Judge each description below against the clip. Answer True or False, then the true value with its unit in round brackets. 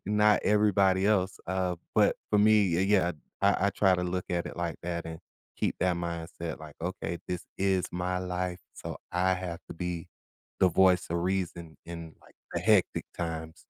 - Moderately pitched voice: False (90 Hz)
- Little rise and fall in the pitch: True (1.9 semitones)